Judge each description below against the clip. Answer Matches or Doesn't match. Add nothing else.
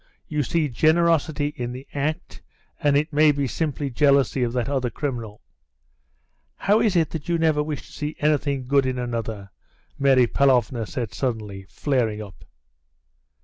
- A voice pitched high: Doesn't match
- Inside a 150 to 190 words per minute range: Matches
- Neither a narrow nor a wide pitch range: Matches